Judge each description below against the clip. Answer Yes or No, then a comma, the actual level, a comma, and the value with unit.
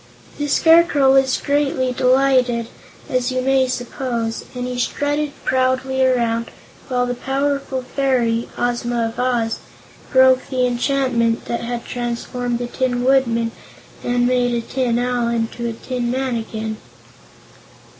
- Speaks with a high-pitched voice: Yes, very high, 250 Hz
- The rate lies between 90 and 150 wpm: Yes, slow, 135 wpm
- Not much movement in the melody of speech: Yes, narrow, 1.8 semitones